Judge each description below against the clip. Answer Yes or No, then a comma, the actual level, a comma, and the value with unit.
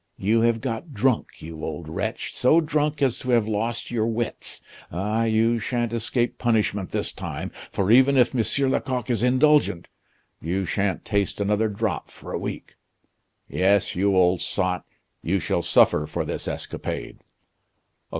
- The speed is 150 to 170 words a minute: Yes, average, 155 wpm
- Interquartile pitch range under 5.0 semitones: Yes, average, 4.1 semitones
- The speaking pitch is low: Yes, low, 110 Hz